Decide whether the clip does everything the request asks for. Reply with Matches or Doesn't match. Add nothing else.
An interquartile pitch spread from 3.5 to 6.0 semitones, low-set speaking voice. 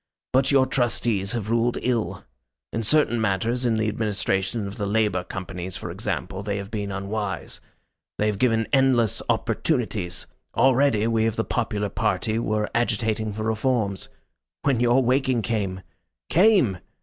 Doesn't match